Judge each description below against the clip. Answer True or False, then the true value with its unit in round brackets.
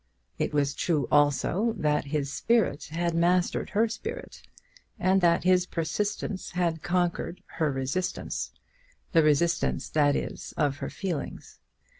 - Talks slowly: True (130 wpm)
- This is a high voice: False (170 Hz)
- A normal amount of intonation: True (3.8 semitones)